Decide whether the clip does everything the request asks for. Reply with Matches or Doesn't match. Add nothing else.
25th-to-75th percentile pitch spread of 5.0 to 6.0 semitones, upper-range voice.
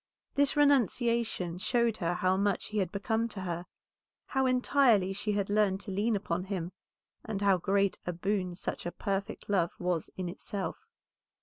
Doesn't match